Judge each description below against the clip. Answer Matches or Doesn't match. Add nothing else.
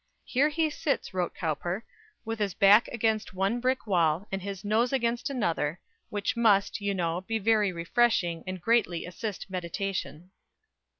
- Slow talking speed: Doesn't match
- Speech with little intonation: Doesn't match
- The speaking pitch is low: Doesn't match